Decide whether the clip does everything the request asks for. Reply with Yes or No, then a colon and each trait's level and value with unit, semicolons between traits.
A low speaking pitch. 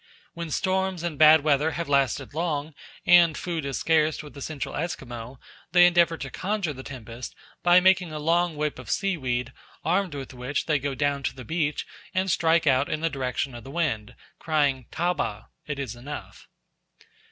No: medium, 150 Hz